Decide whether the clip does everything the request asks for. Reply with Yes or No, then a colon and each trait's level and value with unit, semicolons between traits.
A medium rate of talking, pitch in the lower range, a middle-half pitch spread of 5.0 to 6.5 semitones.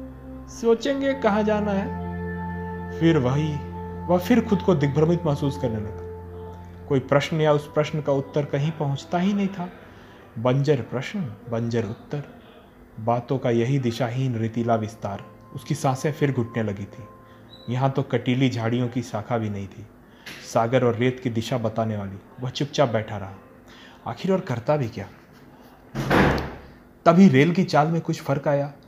Yes: average, 160 wpm; low, 125 Hz; wide, 5.6 semitones